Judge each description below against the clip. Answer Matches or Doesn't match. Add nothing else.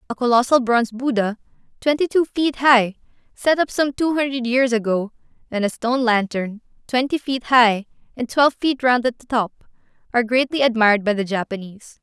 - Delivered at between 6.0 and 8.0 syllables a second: Doesn't match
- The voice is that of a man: Doesn't match